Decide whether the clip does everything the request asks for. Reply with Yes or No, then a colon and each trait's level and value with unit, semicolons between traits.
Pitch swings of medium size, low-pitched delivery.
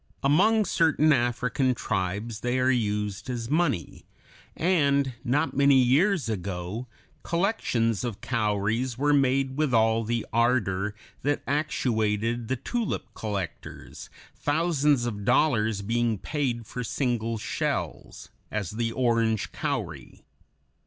Yes: average, 4.4 semitones; low, 120 Hz